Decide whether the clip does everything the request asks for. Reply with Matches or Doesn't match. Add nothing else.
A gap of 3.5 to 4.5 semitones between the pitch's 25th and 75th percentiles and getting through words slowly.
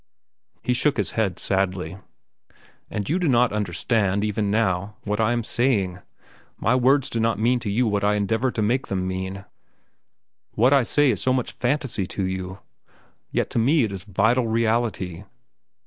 Doesn't match